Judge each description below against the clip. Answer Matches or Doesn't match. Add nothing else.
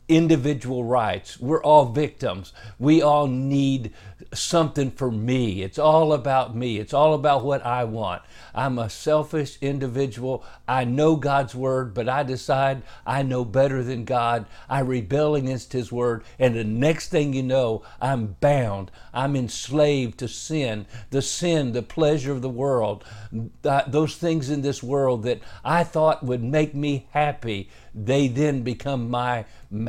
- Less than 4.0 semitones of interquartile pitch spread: Matches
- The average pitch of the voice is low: Matches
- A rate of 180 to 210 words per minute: Doesn't match